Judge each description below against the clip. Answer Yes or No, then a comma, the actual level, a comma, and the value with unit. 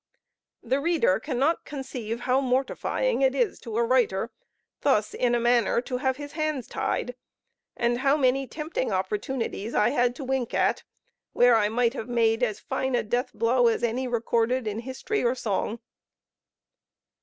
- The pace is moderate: Yes, average, 165 wpm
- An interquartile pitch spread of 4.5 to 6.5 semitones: No, narrow, 2.5 semitones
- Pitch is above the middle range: Yes, high, 245 Hz